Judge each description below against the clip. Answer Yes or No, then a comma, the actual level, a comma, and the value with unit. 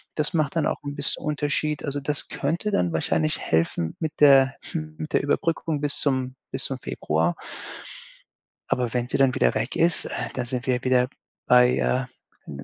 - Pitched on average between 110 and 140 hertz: Yes, low, 135 Hz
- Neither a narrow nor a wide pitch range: Yes, average, 3.3 semitones